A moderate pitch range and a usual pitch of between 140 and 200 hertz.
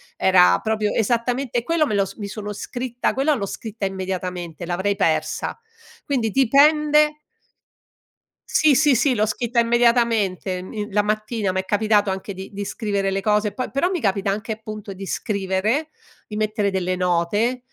No: average, 3.8 semitones; high, 215 Hz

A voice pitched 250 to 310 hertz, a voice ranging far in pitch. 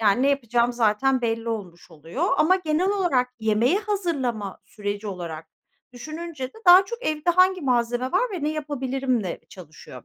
Yes: very high, 255 Hz; wide, 7.3 semitones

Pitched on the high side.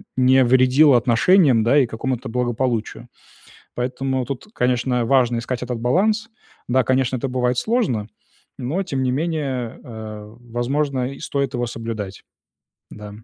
No: low, 125 Hz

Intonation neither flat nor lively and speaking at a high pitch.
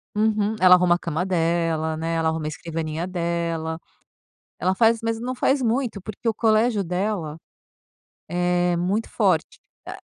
No: average, 4.7 semitones; medium, 180 Hz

